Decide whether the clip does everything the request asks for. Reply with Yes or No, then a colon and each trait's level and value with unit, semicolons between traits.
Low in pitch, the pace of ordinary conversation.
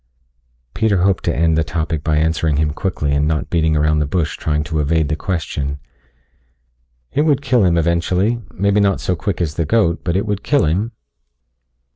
Yes: very low, 85 Hz; average, 190 wpm